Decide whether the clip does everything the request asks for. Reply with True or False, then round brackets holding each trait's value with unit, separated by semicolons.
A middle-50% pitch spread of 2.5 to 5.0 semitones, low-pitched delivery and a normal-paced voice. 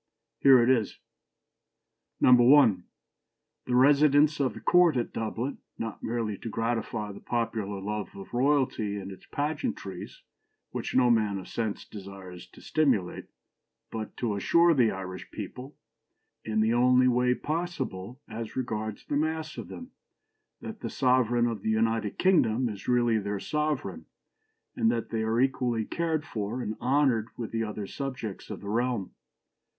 True (3.8 semitones; 120 Hz; 150 wpm)